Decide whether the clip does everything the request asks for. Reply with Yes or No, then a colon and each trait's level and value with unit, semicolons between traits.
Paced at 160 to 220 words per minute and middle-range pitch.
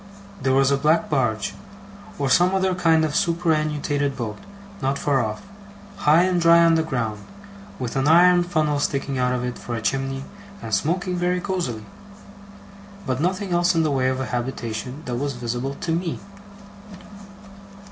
Yes: average, 165 wpm; medium, 145 Hz